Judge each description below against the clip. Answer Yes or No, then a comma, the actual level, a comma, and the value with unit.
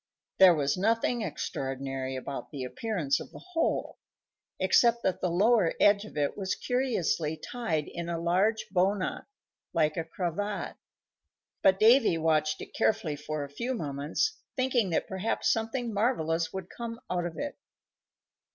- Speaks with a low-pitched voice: No, medium, 185 Hz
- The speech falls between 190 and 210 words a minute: No, average, 150 wpm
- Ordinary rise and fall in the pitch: No, wide, 6.5 semitones